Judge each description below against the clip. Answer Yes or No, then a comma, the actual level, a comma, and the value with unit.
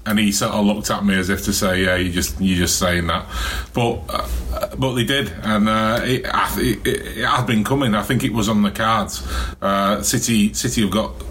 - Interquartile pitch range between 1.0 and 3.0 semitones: No, average, 3.4 semitones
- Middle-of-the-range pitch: No, low, 105 Hz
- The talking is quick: Yes, fast, 235 wpm